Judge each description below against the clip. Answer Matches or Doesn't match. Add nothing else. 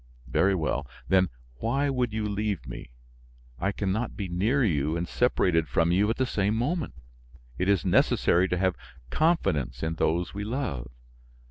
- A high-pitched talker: Doesn't match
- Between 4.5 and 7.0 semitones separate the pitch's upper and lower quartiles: Matches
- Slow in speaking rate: Doesn't match